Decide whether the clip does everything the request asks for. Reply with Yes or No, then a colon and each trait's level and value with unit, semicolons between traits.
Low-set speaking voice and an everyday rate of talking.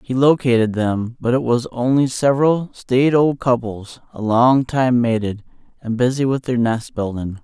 Yes: low, 125 Hz; average, 170 wpm